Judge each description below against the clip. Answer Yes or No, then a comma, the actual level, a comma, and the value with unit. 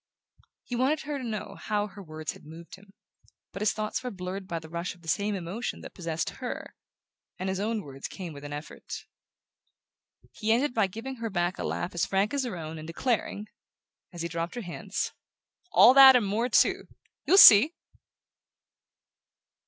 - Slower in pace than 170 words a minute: No, average, 185 wpm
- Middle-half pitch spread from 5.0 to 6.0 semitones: Yes, wide, 5.4 semitones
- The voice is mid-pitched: No, high, 200 Hz